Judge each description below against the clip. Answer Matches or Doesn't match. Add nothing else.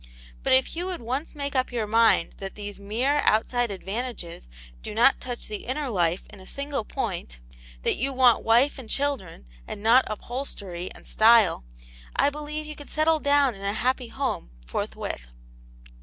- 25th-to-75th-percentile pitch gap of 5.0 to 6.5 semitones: Matches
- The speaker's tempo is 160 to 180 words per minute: Matches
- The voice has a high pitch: Matches